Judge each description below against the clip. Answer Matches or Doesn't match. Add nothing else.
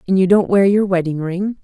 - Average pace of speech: Doesn't match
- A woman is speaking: Matches